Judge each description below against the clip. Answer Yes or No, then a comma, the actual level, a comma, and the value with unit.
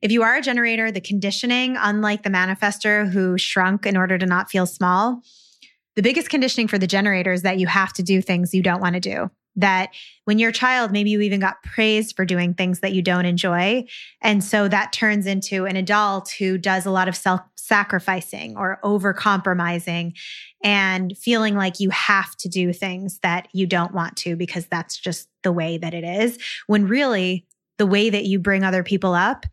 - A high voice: Yes, high, 195 Hz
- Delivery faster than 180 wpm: Yes, fast, 205 wpm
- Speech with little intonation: Yes, narrow, 2.2 semitones